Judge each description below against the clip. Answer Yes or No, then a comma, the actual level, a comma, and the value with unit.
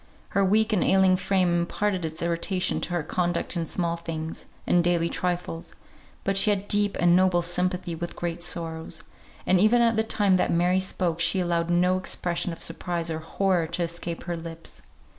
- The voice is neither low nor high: Yes, medium, 175 Hz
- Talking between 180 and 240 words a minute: Yes, average, 185 wpm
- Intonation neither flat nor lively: No, narrow, 1.9 semitones